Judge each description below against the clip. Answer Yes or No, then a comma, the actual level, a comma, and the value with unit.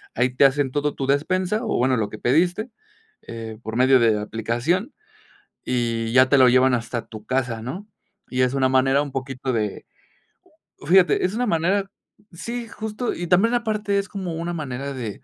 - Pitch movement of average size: No, wide, 6.9 semitones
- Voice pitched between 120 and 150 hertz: Yes, low, 135 Hz